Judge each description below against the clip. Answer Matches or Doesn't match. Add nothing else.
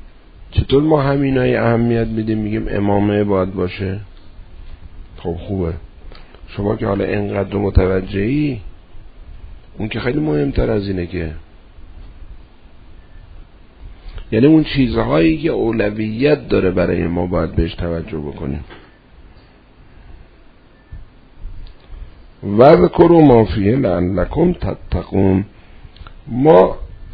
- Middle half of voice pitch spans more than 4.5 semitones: Matches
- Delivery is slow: Matches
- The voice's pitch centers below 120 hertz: Matches